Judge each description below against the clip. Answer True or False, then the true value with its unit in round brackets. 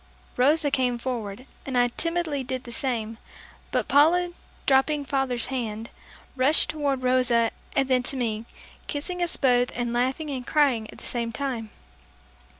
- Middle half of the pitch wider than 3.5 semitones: False (3.0 semitones)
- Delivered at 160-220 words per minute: False (150 wpm)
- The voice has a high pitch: True (255 Hz)